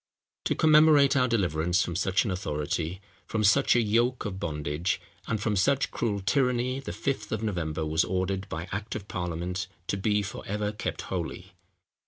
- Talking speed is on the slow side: No, average, 165 wpm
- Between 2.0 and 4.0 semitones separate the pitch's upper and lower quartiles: No, average, 4.7 semitones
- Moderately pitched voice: No, low, 100 Hz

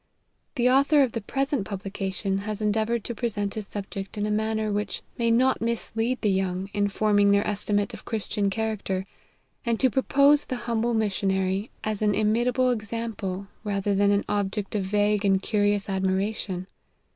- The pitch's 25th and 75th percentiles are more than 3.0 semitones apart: No, narrow, 2.5 semitones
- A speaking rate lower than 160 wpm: No, average, 170 wpm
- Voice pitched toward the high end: Yes, high, 210 Hz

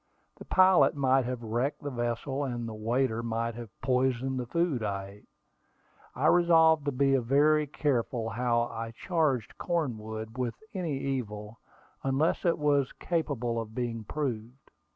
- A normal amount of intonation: Yes, average, 3.8 semitones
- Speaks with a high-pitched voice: No, low, 125 Hz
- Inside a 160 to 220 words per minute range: No, average, 150 wpm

